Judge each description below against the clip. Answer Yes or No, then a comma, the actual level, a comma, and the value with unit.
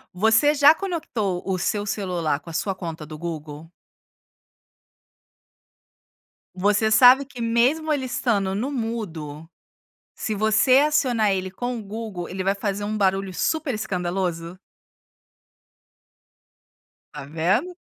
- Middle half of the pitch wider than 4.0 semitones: Yes, average, 5.3 semitones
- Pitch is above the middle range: Yes, high, 205 Hz